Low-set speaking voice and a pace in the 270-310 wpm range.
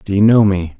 Yes: low, 100 Hz; fast, 305 wpm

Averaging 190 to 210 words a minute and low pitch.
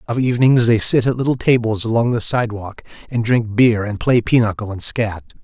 Yes: average, 200 wpm; low, 115 Hz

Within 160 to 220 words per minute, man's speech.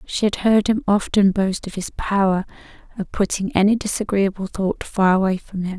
No: average, 185 wpm; female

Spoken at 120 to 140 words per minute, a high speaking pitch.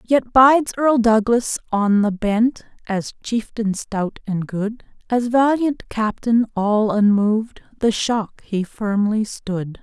Yes: slow, 135 wpm; high, 220 Hz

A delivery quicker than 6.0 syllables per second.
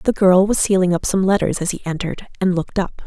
Yes: 6.5 syllables/s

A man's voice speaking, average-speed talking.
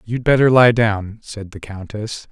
Yes: male; average, 180 wpm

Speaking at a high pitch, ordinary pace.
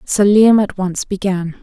Yes: high, 195 Hz; average, 150 wpm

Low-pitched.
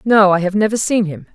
No: high, 205 Hz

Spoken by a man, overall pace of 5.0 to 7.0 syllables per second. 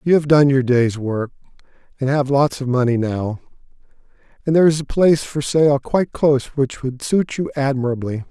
Yes: male; 5.4 syllables/s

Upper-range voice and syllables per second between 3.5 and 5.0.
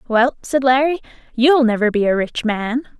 Yes: high, 245 Hz; 4.7 syllables/s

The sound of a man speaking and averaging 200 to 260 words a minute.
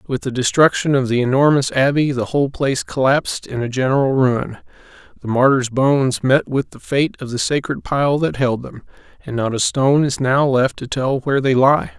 Yes: male; fast, 205 wpm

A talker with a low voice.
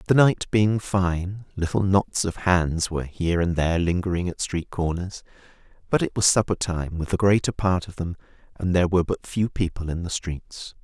Yes: very low, 90 Hz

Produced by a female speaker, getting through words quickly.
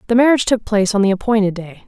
Yes: female; fast, 255 wpm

